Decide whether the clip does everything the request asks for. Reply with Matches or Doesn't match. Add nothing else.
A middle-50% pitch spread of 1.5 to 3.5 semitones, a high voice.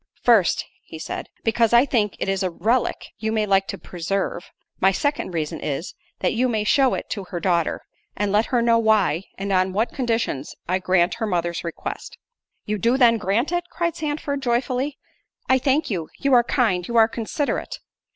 Doesn't match